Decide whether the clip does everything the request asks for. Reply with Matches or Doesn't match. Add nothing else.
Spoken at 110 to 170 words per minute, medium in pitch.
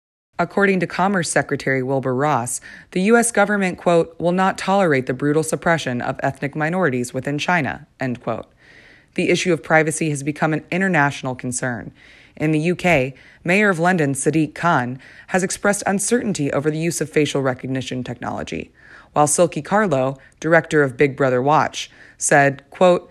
Matches